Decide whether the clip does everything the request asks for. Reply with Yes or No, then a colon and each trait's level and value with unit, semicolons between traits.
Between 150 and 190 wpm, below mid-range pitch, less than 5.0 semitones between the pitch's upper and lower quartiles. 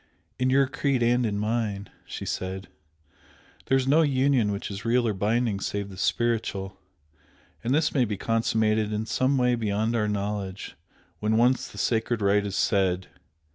Yes: average, 170 wpm; low, 110 Hz; average, 3.4 semitones